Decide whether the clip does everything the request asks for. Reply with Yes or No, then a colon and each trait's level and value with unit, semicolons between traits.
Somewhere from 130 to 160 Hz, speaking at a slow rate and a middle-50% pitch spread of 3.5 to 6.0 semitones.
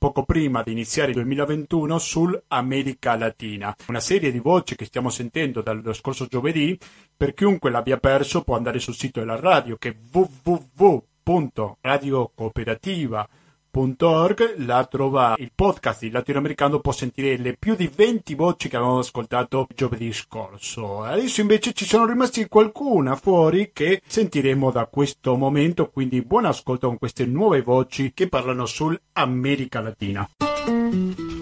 No: low, 135 Hz; average, 140 wpm; average, 5.3 semitones